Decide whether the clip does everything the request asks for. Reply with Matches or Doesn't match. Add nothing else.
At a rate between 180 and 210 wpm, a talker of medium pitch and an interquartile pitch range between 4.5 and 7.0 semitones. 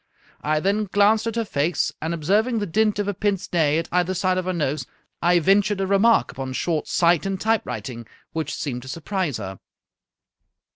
Matches